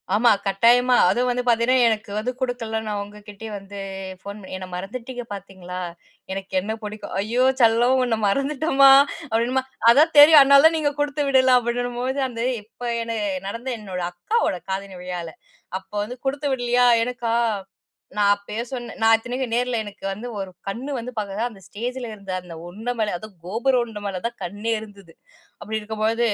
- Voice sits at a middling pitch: No, high, 230 Hz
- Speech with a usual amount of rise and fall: Yes, average, 3.5 semitones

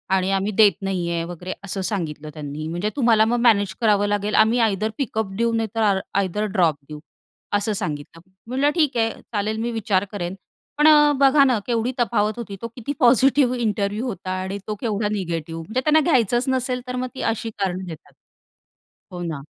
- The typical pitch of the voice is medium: No, high, 210 Hz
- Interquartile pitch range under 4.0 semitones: No, average, 4.3 semitones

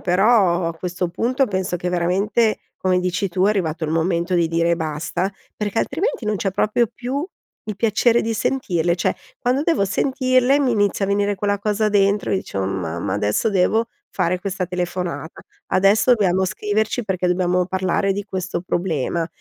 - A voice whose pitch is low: No, high, 190 Hz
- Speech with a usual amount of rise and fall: Yes, average, 3.3 semitones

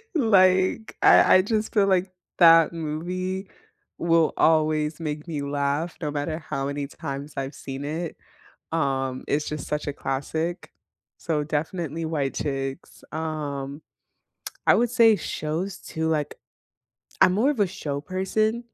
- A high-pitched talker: No, medium, 160 Hz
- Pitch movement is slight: No, average, 4.1 semitones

